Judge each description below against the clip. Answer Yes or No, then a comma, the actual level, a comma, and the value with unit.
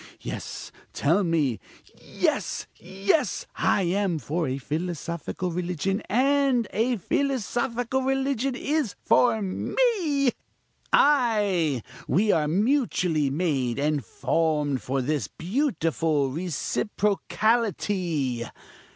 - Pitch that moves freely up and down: Yes, wide, 8.0 semitones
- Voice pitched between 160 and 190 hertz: Yes, medium, 185 Hz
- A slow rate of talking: Yes, slow, 90 wpm